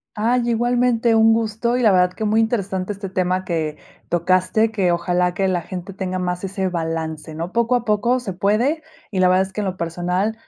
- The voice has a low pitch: No, high, 190 Hz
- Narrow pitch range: No, average, 3.7 semitones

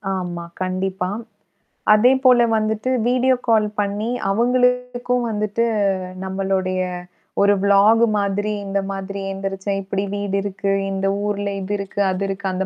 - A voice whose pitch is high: Yes, high, 200 Hz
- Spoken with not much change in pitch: Yes, narrow, 2.2 semitones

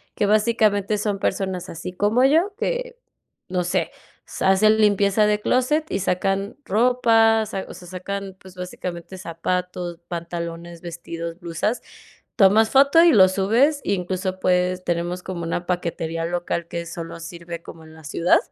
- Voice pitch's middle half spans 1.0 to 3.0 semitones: No, average, 3.7 semitones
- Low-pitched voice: No, medium, 185 Hz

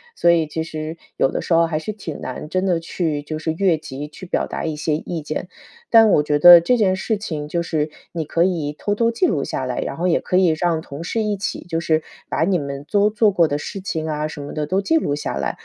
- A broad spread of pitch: No, average, 3.6 semitones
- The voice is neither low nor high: Yes, medium, 165 Hz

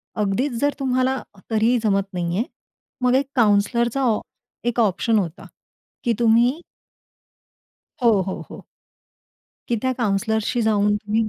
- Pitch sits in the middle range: No, high, 225 Hz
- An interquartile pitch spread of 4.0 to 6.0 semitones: No, average, 3.2 semitones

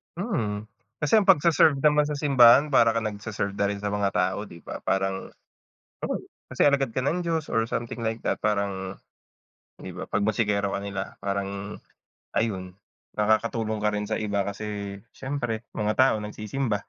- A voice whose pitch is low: Yes, low, 110 Hz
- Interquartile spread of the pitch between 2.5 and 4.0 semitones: No, average, 4.5 semitones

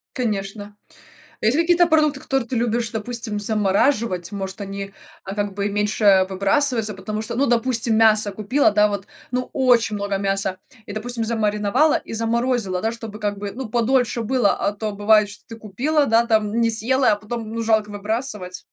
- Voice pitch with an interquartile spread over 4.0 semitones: No, average, 2.8 semitones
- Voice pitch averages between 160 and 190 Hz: No, high, 220 Hz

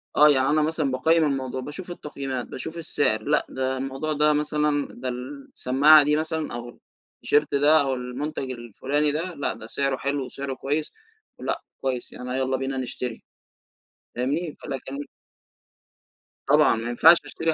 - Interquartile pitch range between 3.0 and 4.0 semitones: No, narrow, 2.6 semitones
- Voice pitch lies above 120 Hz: Yes, medium, 140 Hz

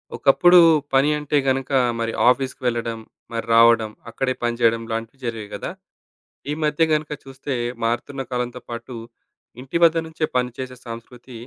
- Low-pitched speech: Yes, low, 125 Hz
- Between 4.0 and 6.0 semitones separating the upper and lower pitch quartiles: No, average, 2.8 semitones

